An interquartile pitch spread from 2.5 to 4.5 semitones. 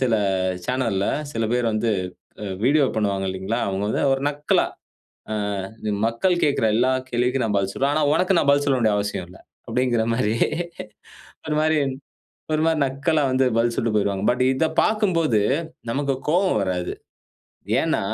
No: average, 5.3 semitones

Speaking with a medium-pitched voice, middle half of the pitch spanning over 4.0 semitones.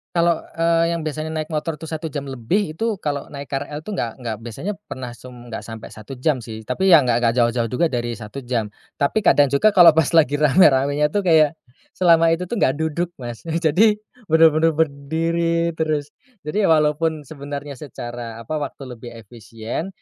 Yes: medium, 150 Hz; average, 4.7 semitones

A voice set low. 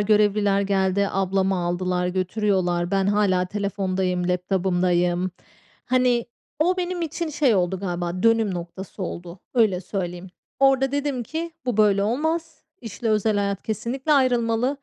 No: high, 200 Hz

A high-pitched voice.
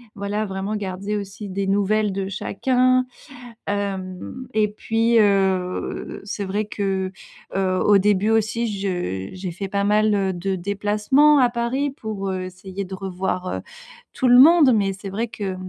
Yes: high, 200 Hz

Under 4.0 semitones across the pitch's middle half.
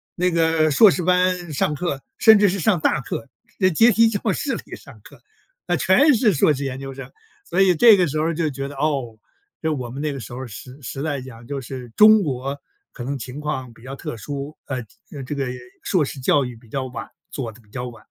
No: average, 5.3 semitones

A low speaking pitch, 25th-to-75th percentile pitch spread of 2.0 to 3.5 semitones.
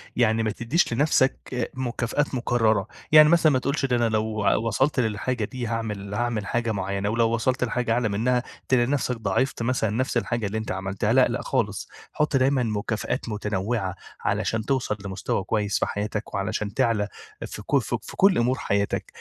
Yes: low, 115 Hz; average, 3.2 semitones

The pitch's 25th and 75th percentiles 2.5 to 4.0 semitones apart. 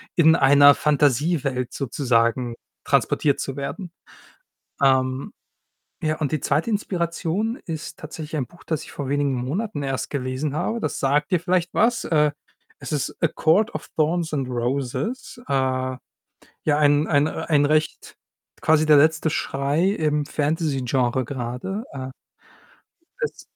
Yes: average, 3.4 semitones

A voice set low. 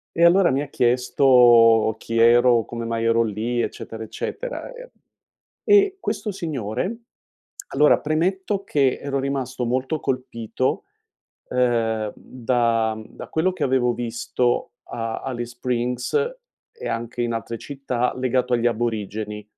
Yes: low, 125 Hz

